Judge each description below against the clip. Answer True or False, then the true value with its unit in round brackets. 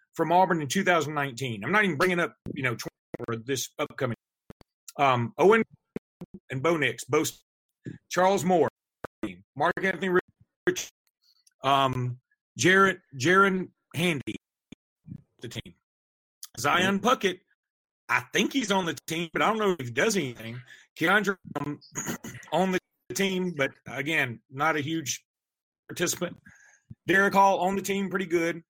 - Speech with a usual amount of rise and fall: False (6.1 semitones)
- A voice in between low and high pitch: True (165 Hz)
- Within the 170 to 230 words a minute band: False (135 wpm)